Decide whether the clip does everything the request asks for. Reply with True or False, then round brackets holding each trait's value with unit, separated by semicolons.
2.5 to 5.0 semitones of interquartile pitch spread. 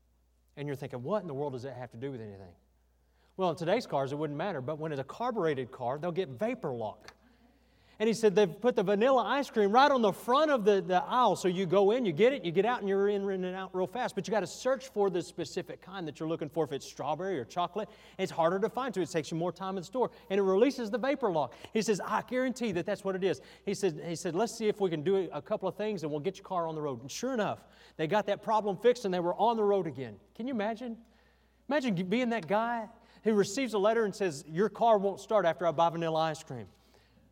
False (5.4 semitones)